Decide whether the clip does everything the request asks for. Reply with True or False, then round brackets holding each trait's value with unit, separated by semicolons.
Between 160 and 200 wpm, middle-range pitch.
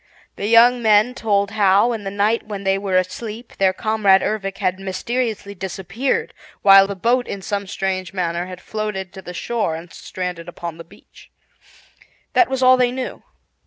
False (175 wpm; 200 Hz)